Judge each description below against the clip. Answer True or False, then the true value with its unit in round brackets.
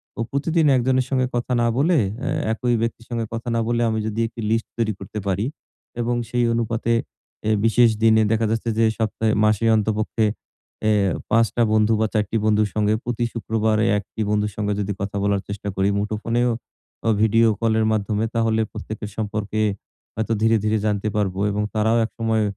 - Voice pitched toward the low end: True (110 Hz)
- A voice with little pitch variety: True (1.5 semitones)